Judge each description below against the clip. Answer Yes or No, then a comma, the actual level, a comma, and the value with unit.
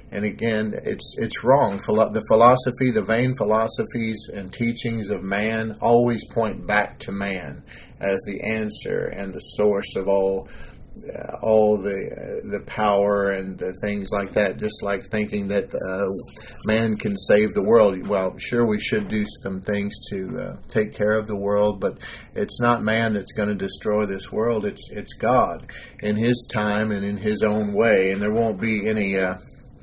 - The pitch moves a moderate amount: No, narrow, 2.0 semitones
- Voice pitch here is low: Yes, low, 105 Hz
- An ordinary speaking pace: Yes, average, 180 wpm